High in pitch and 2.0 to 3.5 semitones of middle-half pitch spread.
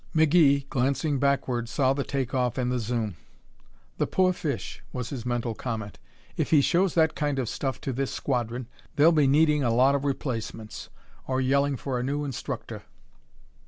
No: low, 135 Hz; average, 2.7 semitones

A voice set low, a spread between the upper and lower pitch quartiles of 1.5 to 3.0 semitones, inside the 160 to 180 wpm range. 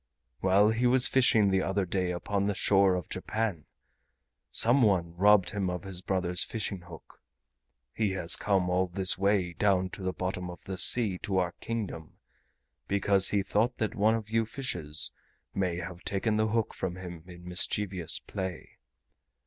Yes: very low, 95 Hz; average, 2.7 semitones; average, 170 wpm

